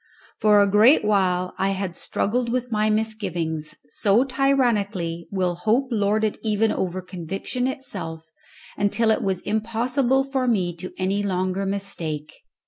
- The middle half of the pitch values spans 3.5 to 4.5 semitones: Yes, average, 3.9 semitones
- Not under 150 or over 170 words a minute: No, average, 140 wpm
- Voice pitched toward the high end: Yes, high, 205 Hz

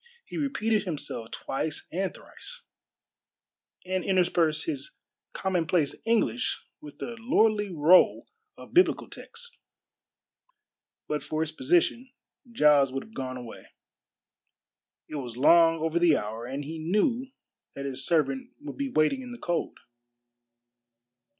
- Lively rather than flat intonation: Yes, wide, 7.4 semitones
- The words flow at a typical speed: No, slow, 130 wpm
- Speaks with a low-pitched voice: No, medium, 170 Hz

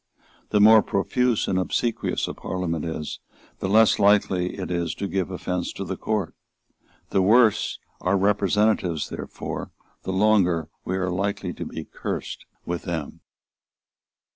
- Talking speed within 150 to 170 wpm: No, average, 140 wpm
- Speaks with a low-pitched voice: Yes, very low, 95 Hz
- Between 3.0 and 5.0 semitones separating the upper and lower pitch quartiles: No, narrow, 2.6 semitones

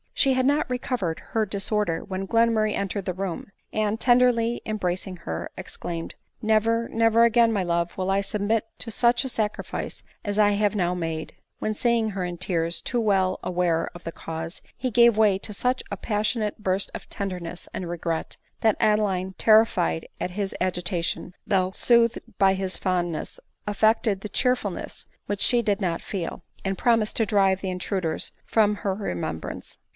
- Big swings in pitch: No, average, 3.5 semitones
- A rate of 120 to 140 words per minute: No, average, 175 wpm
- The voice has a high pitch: Yes, high, 200 Hz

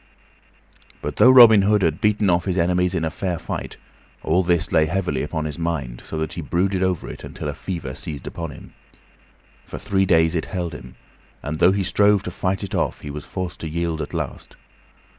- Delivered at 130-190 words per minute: No, fast, 205 wpm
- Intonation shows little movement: No, average, 3.3 semitones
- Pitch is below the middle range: Yes, very low, 85 Hz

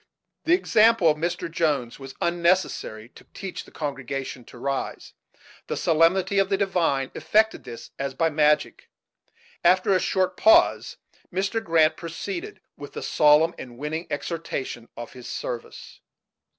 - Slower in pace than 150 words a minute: Yes, average, 140 wpm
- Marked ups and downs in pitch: Yes, wide, 5.7 semitones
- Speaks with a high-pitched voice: No, medium, 165 Hz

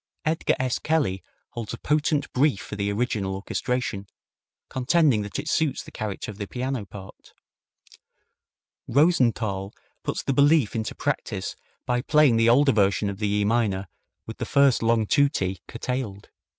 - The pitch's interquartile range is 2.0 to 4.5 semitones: No, average, 5.3 semitones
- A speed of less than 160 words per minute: Yes, average, 150 wpm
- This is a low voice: Yes, low, 115 Hz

